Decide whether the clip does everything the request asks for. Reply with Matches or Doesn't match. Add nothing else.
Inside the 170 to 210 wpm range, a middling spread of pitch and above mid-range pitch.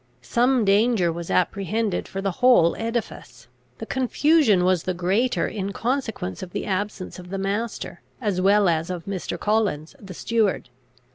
Doesn't match